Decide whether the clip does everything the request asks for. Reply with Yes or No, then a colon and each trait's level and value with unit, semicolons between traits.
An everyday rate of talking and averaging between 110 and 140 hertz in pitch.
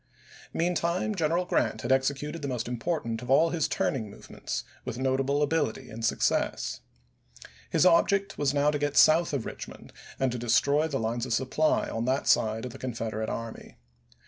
Yes: average, 170 wpm; low, 135 Hz